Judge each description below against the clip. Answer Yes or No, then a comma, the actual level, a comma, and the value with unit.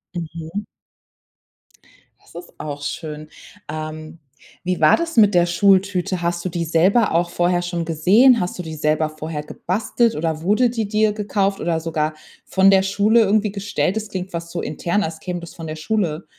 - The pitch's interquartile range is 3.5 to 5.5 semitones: Yes, average, 4.0 semitones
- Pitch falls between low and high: Yes, medium, 175 Hz